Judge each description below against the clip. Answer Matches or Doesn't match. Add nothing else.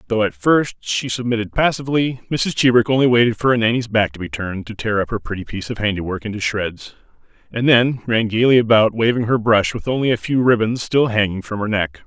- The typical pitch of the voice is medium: Doesn't match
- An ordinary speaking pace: Doesn't match